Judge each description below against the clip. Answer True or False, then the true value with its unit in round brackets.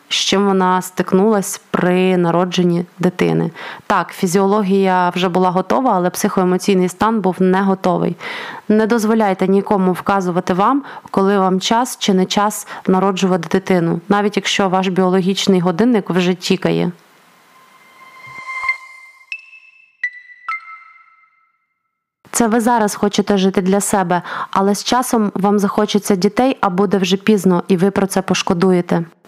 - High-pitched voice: True (200 Hz)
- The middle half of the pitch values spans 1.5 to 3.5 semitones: False (4.0 semitones)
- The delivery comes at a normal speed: True (125 wpm)